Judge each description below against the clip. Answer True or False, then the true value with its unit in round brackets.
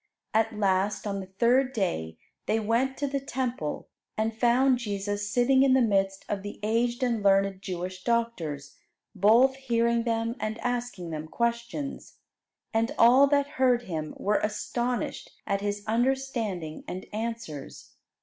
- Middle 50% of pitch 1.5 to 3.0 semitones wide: False (3.7 semitones)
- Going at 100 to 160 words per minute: True (145 wpm)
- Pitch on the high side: True (225 Hz)